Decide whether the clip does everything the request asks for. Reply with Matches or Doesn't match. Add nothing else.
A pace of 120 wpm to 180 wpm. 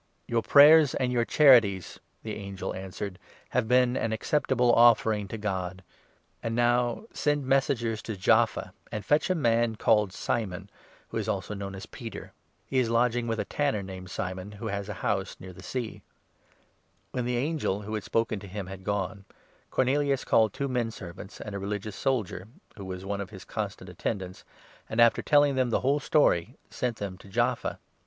Doesn't match